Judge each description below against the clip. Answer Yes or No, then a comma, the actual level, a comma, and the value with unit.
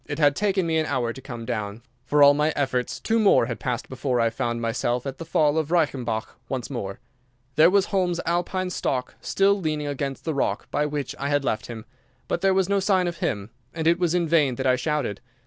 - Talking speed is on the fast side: Yes, fast, 230 wpm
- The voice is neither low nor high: Yes, medium, 145 Hz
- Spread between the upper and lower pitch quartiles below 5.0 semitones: No, wide, 5.5 semitones